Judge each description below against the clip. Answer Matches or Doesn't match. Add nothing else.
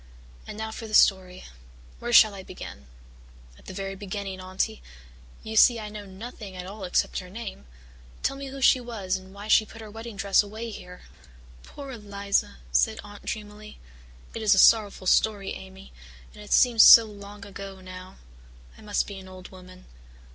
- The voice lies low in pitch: Doesn't match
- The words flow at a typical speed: Matches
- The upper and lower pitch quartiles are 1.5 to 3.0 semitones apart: Matches